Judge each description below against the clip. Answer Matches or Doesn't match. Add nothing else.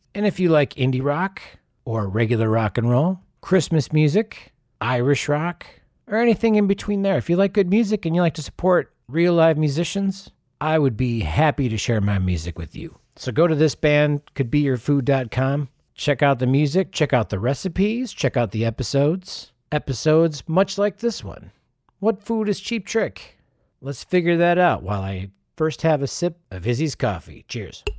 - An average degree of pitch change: Doesn't match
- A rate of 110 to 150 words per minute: Doesn't match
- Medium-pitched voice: Matches